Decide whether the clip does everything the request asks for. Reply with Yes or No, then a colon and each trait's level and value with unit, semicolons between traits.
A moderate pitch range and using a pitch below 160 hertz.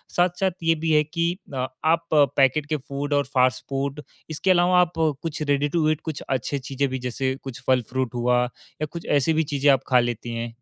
Yes: average, 3.6 semitones; medium, 140 Hz